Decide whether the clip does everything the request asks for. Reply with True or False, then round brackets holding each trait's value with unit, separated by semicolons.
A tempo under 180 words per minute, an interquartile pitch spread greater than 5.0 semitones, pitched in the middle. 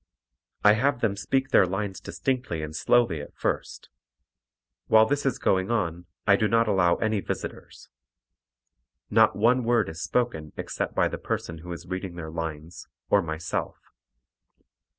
False (150 wpm; 5.6 semitones; 95 Hz)